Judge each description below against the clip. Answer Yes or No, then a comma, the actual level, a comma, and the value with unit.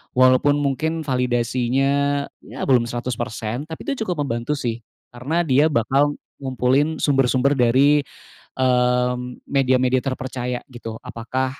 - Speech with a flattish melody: Yes, narrow, 2.3 semitones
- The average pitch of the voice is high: No, low, 130 Hz